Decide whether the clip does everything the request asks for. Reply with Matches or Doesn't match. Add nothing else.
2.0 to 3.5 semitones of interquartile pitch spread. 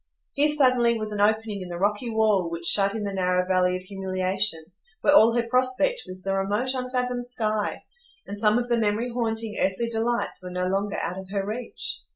Doesn't match